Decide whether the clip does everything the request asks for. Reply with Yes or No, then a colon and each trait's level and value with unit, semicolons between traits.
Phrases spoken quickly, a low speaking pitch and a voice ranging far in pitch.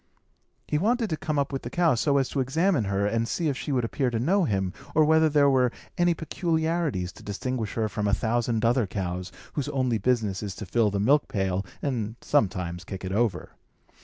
Yes: fast, 215 wpm; low, 120 Hz; wide, 6.5 semitones